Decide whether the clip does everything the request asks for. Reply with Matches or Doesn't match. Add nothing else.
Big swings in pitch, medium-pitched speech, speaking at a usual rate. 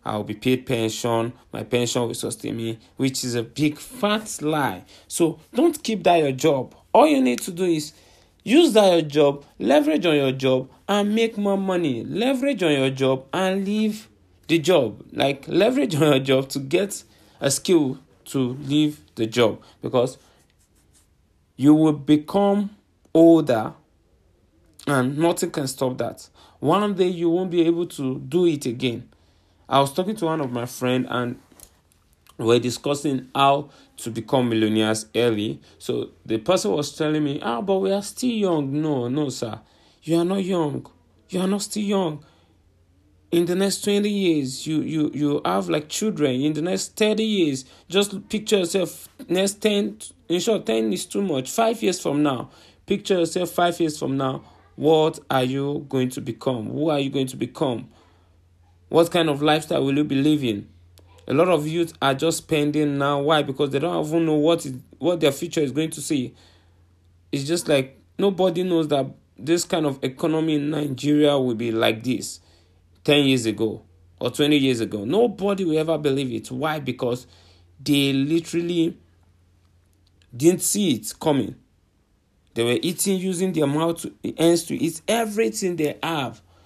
Matches